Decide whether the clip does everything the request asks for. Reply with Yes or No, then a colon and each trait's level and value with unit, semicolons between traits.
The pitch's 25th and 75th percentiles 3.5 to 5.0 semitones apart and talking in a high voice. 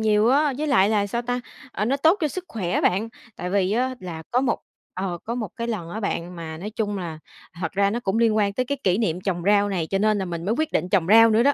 Yes: average, 4.3 semitones; high, 210 Hz